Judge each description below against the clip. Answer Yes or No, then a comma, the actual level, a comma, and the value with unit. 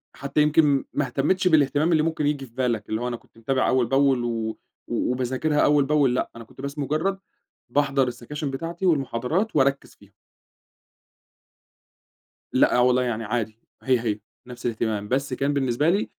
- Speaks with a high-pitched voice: No, low, 135 Hz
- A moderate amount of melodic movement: Yes, average, 3.5 semitones